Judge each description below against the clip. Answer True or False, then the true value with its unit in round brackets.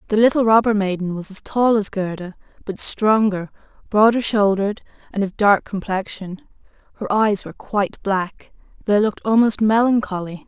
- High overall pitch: True (205 Hz)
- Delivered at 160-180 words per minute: False (150 wpm)